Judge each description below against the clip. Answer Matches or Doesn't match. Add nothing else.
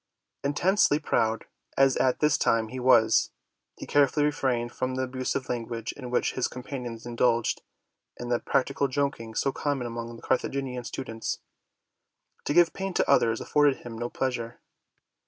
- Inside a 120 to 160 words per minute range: Matches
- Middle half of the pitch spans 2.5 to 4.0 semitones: Matches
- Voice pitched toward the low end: Matches